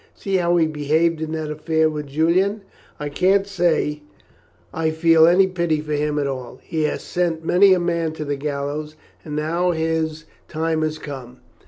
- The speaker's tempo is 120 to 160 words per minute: No, average, 180 wpm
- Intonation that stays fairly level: Yes, narrow, 2.2 semitones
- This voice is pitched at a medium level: Yes, medium, 160 Hz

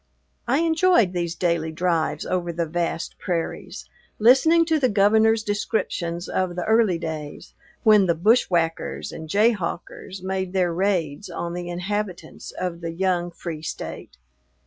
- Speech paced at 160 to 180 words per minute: No, average, 140 wpm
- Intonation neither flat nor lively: Yes, average, 3.7 semitones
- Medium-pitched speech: Yes, medium, 180 Hz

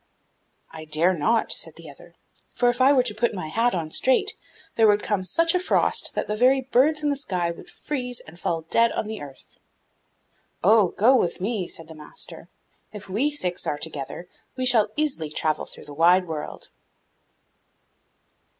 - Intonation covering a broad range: Yes, wide, 7.1 semitones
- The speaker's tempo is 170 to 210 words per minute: Yes, average, 185 wpm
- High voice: Yes, high, 210 Hz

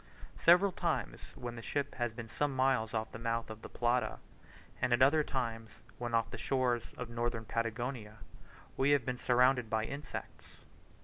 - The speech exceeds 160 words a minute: Yes, average, 175 wpm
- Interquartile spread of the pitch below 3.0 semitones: Yes, narrow, 2.4 semitones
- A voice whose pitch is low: Yes, low, 120 Hz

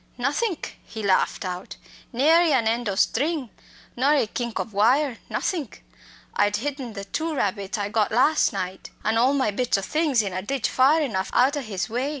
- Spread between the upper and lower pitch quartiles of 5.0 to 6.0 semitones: Yes, wide, 5.6 semitones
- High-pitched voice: Yes, high, 240 Hz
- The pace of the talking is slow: No, average, 190 wpm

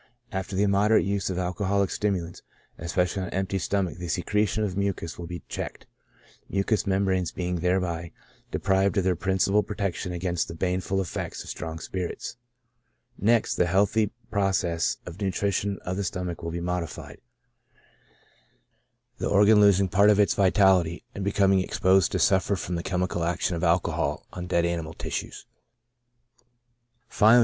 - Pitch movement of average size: No, narrow, 2.1 semitones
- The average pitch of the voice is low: Yes, very low, 95 Hz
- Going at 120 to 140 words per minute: No, average, 155 wpm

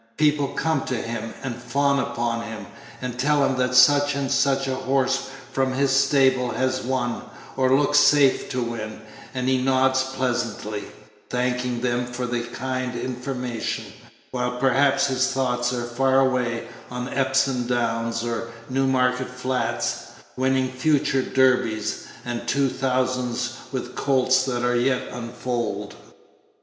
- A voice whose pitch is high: No, low, 130 Hz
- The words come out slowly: No, average, 145 wpm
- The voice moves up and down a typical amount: No, narrow, 1.6 semitones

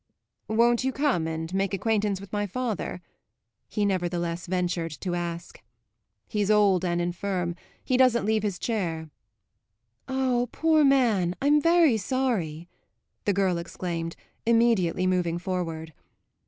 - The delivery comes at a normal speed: No, slow, 125 wpm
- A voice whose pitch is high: Yes, high, 195 Hz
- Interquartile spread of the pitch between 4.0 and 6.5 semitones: Yes, average, 5.2 semitones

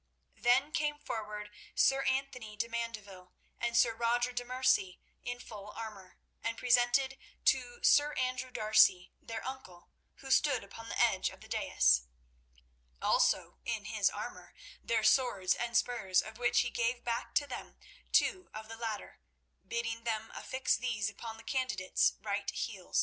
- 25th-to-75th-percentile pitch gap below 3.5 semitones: Yes, average, 2.9 semitones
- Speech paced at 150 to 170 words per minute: Yes, average, 155 wpm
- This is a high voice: Yes, high, 235 Hz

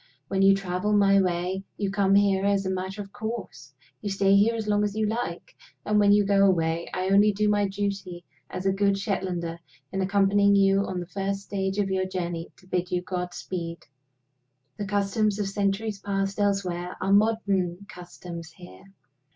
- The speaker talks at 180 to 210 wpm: Yes, average, 185 wpm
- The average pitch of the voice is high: Yes, high, 195 Hz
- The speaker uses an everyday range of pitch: No, narrow, 1.8 semitones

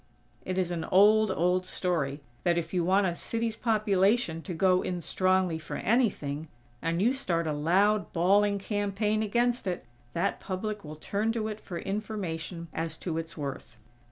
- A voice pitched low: No, medium, 185 Hz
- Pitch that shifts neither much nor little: Yes, average, 3.9 semitones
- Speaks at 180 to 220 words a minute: No, average, 170 wpm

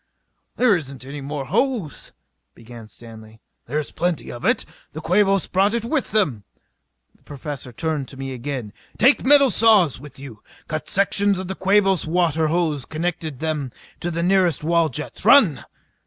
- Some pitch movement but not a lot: No, wide, 5.9 semitones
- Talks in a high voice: No, medium, 160 Hz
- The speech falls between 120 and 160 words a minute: No, average, 170 wpm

